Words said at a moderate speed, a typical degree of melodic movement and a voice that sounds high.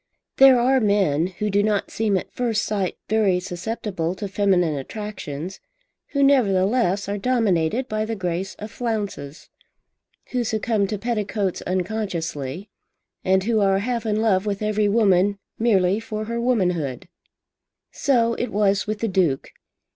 Yes: average, 145 wpm; average, 3.1 semitones; high, 205 Hz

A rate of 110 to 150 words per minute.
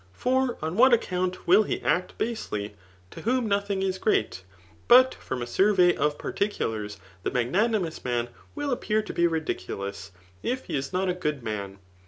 No: average, 170 wpm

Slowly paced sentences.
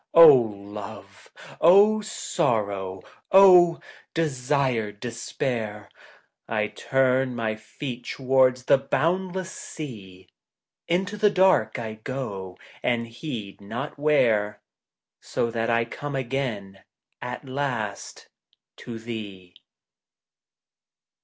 Yes: slow, 90 wpm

